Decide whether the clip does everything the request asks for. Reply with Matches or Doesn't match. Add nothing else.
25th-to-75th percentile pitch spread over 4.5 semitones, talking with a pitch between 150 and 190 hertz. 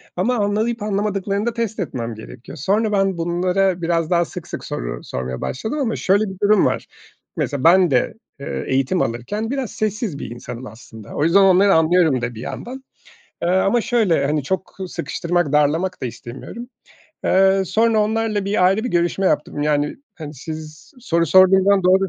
Matches